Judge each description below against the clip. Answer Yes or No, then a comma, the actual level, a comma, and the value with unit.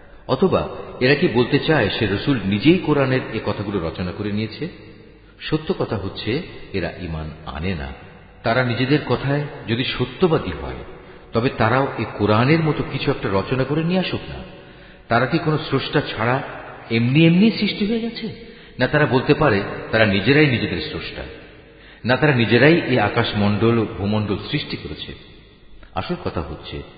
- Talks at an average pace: No, fast, 150 wpm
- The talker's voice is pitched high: No, low, 120 Hz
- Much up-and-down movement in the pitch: Yes, wide, 6.5 semitones